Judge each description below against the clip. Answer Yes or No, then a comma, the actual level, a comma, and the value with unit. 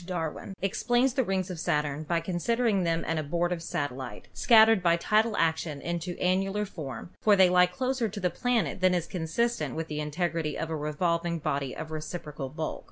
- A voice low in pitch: No, medium, 170 Hz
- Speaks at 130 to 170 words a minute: No, average, 185 wpm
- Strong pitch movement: No, average, 3.8 semitones